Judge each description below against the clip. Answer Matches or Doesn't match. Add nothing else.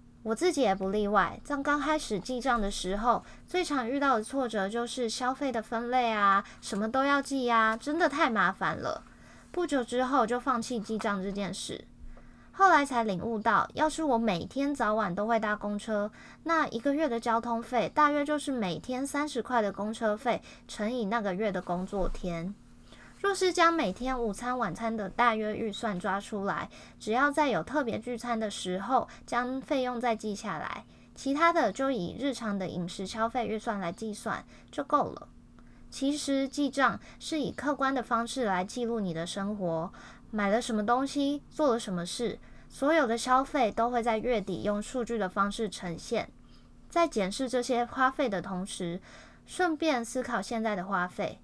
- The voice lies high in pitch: Matches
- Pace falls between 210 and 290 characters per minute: Matches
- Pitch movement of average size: Matches